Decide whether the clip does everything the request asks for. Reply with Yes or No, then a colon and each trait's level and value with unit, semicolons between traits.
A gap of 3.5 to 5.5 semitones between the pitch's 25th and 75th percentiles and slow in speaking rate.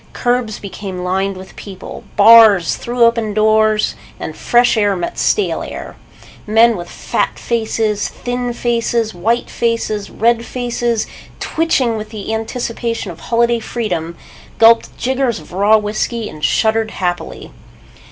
No: narrow, 2.5 semitones; slow, 130 wpm